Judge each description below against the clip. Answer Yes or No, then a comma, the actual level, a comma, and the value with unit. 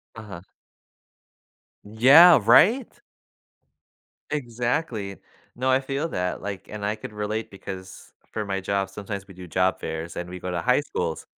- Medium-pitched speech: No, low, 105 Hz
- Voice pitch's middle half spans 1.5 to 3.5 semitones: No, average, 5.0 semitones